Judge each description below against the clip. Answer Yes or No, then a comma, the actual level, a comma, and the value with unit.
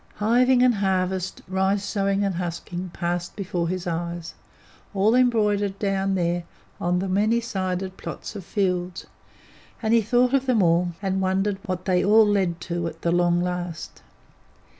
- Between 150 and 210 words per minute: Yes, average, 160 wpm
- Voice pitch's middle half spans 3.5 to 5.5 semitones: No, average, 2.8 semitones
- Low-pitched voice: No, high, 190 Hz